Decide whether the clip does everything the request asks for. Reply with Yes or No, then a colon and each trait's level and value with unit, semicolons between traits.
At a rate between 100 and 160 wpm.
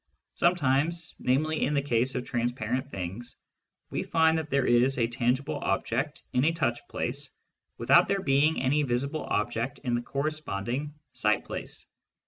Yes: average, 150 wpm